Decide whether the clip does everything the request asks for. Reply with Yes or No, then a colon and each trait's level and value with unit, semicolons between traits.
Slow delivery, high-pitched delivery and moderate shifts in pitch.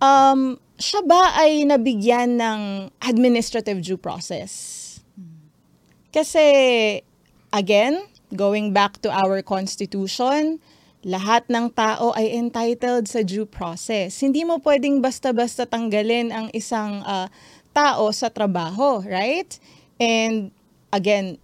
Yes: slow, 105 wpm; high, 225 Hz; average, 4.3 semitones